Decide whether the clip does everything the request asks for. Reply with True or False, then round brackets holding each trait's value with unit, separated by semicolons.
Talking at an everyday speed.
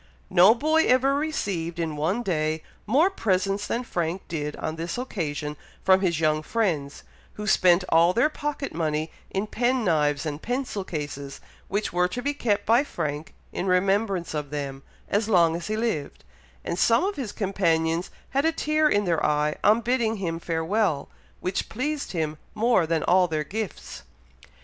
True (170 wpm)